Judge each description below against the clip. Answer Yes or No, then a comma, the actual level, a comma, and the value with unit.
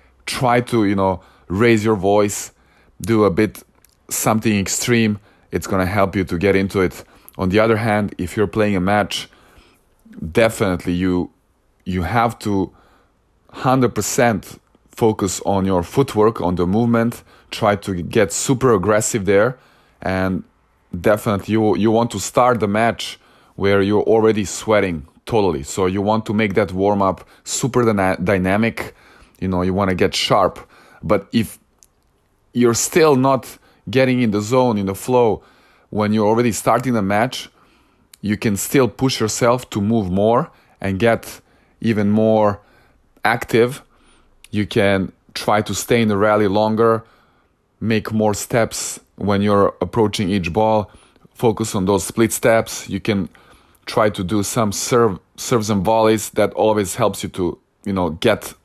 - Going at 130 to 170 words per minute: Yes, average, 155 wpm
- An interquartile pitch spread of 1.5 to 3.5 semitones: Yes, average, 2.7 semitones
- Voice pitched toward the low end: Yes, low, 105 Hz